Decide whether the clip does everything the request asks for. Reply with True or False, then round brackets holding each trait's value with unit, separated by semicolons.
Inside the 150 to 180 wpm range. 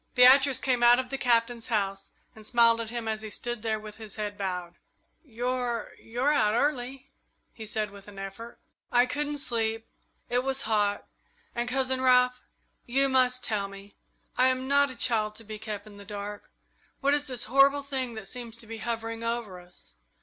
False (190 wpm)